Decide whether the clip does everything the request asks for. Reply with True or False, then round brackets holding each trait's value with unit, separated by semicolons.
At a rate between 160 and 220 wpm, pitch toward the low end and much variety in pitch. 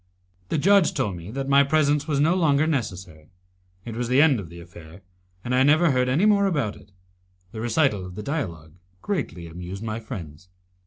True (195 wpm; 125 Hz; 8.3 semitones)